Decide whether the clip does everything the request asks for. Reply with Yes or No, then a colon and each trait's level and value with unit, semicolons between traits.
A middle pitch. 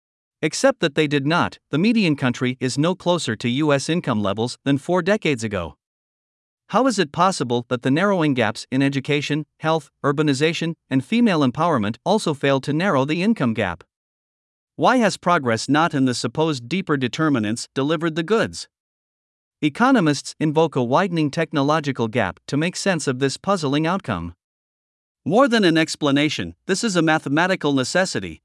Yes: medium, 150 Hz